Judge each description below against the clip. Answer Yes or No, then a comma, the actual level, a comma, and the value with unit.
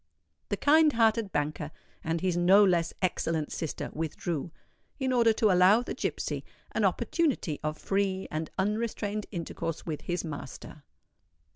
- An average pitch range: Yes, average, 5.0 semitones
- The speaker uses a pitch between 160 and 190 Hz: Yes, medium, 185 Hz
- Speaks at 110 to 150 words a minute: Yes, average, 140 wpm